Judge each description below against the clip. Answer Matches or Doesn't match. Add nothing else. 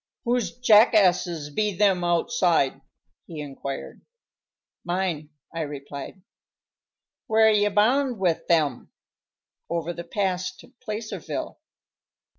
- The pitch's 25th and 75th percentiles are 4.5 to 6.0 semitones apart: Matches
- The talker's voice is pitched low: Doesn't match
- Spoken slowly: Matches